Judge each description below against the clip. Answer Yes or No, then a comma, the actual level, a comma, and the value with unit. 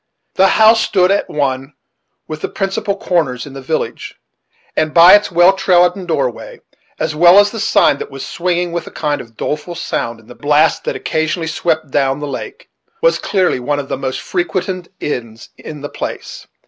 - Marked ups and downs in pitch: No, average, 4.6 semitones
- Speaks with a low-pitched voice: No, medium, 160 Hz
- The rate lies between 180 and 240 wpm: Yes, average, 185 wpm